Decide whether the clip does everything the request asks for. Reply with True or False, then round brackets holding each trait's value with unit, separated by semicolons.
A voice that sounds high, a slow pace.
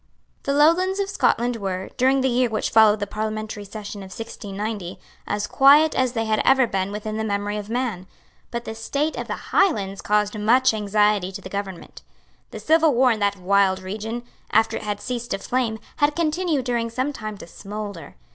False (220 Hz; 195 wpm)